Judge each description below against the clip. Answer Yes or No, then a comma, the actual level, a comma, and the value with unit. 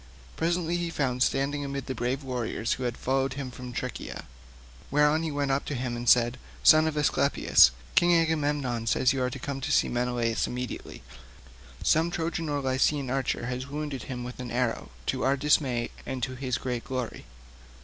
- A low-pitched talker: Yes, low, 130 Hz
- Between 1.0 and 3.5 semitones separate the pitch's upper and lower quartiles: Yes, average, 2.9 semitones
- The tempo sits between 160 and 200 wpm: Yes, average, 190 wpm